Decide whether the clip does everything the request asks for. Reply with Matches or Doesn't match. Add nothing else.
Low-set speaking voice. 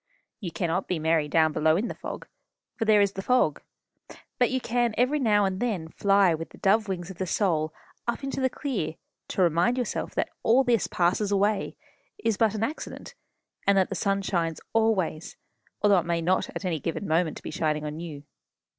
Doesn't match